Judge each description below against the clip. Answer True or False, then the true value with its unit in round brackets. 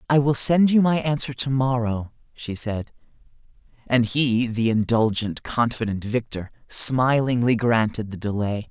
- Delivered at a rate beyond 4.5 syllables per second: False (4.3 syllables/s)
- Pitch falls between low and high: False (120 Hz)